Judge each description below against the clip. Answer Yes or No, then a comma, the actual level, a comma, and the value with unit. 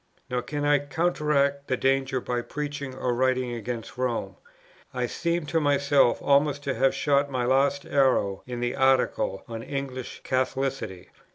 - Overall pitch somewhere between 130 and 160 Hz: Yes, low, 135 Hz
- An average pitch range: No, narrow, 2.3 semitones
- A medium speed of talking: Yes, average, 155 wpm